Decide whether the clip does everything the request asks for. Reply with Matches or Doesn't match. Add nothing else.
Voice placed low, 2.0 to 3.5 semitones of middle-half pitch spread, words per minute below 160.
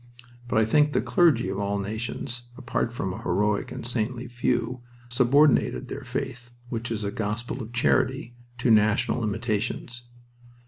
Matches